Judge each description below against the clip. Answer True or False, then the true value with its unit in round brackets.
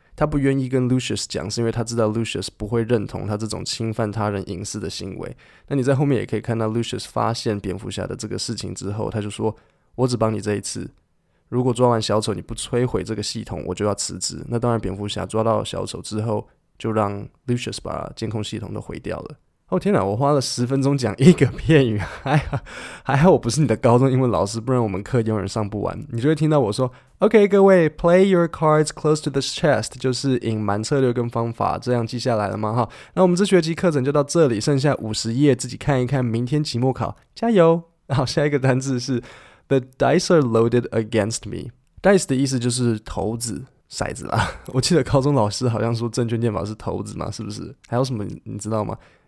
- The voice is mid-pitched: False (120 Hz)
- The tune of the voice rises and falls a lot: False (4.1 semitones)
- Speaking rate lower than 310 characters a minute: False (395 characters per minute)